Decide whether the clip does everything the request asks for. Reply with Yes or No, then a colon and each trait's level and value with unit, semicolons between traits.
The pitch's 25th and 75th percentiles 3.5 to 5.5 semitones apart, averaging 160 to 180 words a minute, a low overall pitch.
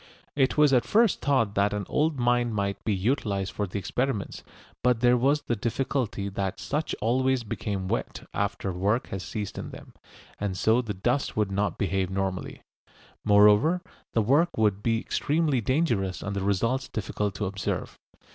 Yes: average, 4.6 semitones; average, 170 wpm; low, 110 Hz